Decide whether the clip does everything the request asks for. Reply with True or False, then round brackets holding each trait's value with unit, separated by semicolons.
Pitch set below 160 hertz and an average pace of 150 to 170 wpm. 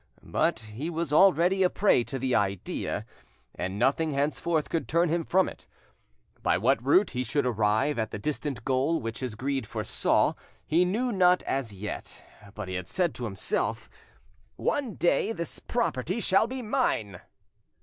True (140 Hz; 165 wpm)